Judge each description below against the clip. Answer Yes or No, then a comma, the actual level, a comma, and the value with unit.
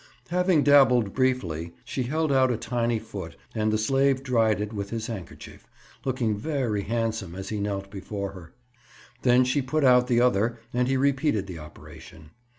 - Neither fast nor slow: Yes, average, 170 wpm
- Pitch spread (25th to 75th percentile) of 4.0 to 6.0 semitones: Yes, average, 4.4 semitones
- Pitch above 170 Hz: No, low, 115 Hz